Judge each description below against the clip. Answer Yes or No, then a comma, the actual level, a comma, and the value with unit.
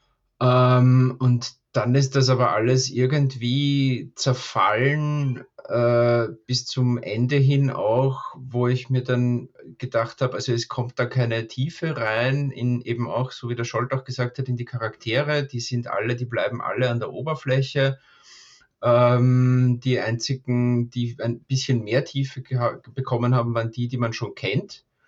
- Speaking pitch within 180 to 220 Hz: No, low, 125 Hz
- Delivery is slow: No, average, 150 wpm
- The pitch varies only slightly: Yes, narrow, 1.7 semitones